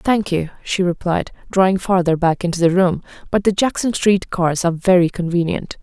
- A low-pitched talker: No, medium, 180 Hz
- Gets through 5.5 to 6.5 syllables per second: No, 5.2 syllables/s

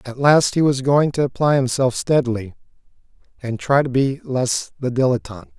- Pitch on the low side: Yes, low, 130 Hz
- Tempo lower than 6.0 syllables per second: Yes, 5.1 syllables/s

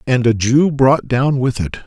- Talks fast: Yes, fast, 225 wpm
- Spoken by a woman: No, male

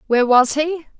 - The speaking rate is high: No, average, 180 wpm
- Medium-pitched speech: No, very high, 280 Hz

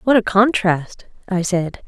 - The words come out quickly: No, average, 160 wpm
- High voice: Yes, high, 200 Hz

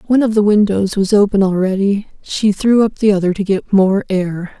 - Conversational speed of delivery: No, fast, 210 wpm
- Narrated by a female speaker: Yes, female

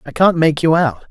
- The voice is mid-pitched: Yes, medium, 155 Hz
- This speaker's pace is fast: Yes, fast, 270 wpm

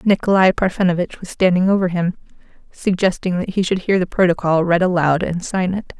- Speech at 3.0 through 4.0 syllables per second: No, 5.6 syllables/s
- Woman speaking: Yes, female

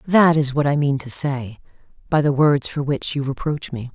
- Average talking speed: No, fast, 230 wpm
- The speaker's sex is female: Yes, female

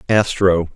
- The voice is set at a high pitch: No, very low, 95 Hz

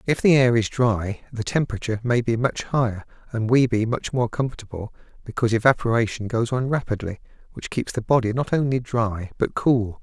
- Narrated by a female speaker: No, male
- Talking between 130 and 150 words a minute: No, average, 185 wpm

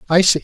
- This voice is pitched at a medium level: Yes, medium, 180 Hz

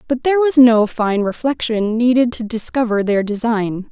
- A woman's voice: Yes, female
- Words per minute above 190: No, average, 170 wpm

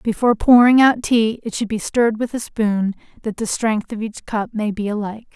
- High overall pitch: Yes, high, 220 Hz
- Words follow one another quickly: Yes, fast, 225 wpm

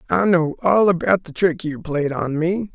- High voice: No, medium, 170 Hz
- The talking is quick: Yes, fast, 220 wpm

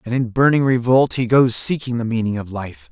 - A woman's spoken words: No, male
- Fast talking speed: Yes, fast, 225 wpm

